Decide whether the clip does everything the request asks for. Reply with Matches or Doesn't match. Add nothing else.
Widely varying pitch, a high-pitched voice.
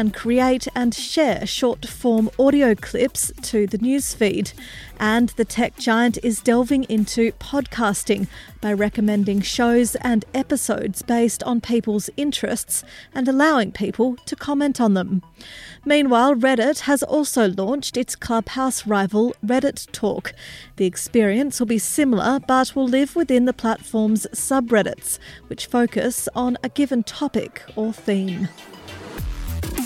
Doesn't match